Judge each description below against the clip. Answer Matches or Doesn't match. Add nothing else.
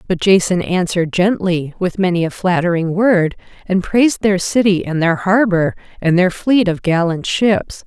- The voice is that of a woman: Matches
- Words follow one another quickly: Doesn't match